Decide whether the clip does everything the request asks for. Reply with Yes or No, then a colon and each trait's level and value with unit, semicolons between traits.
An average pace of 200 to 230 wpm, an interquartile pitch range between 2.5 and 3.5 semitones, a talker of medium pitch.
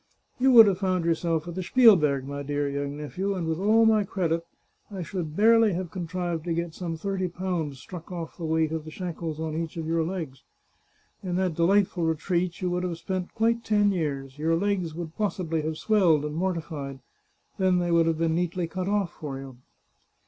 Yes: fast, 205 wpm; average, 2.8 semitones; medium, 170 Hz